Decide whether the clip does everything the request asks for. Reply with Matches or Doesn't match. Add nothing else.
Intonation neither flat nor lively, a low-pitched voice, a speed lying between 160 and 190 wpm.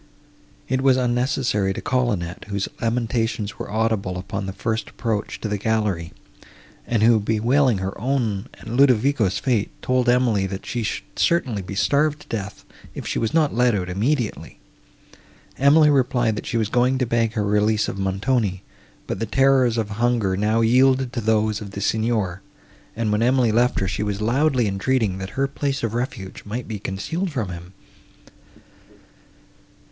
Matches